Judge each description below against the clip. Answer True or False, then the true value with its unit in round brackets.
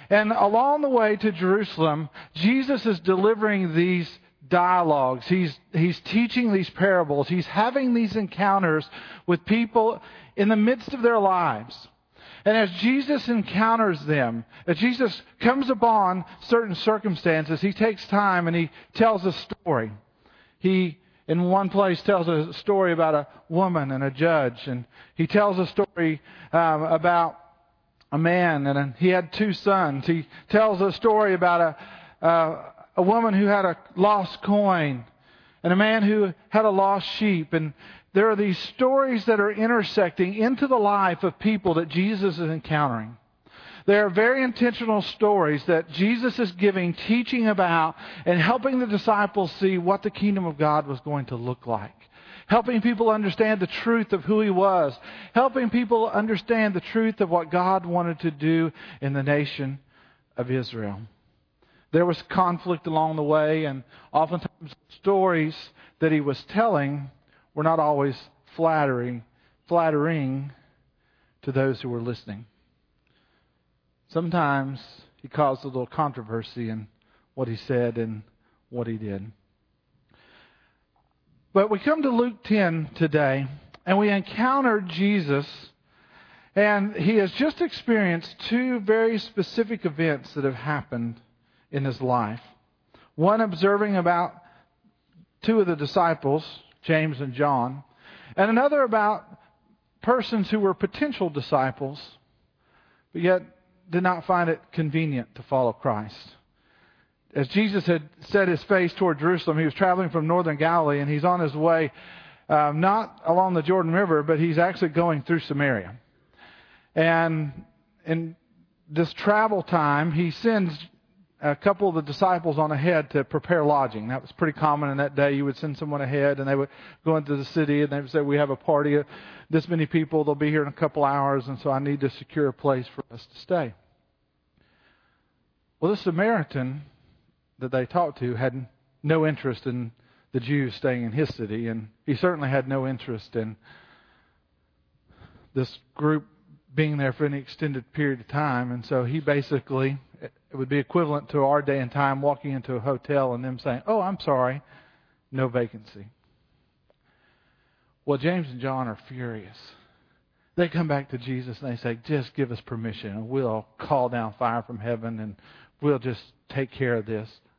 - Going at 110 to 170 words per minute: True (160 wpm)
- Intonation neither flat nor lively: False (6.2 semitones)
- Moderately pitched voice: True (160 Hz)